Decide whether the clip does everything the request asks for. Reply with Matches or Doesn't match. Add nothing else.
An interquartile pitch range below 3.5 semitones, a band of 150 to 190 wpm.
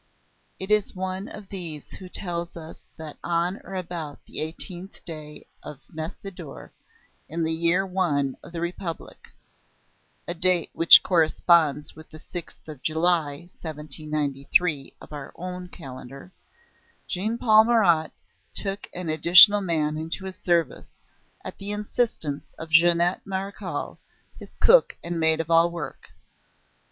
Doesn't match